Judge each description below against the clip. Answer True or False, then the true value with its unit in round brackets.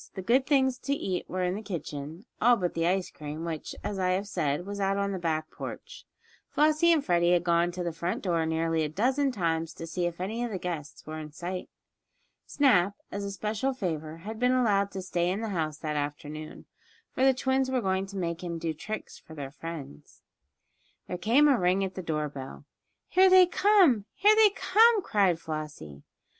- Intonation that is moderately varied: False (6.1 semitones)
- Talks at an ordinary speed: False (210 wpm)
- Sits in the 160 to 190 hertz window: True (185 Hz)